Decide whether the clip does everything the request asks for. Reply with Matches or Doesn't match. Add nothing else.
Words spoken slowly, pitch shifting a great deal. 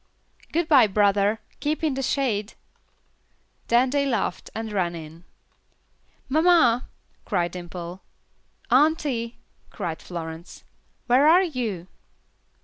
Matches